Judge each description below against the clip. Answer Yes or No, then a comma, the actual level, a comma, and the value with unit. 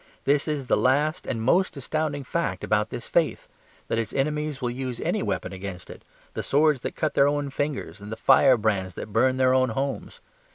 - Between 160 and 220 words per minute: Yes, average, 200 wpm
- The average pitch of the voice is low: Yes, low, 130 Hz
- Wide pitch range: No, average, 4.6 semitones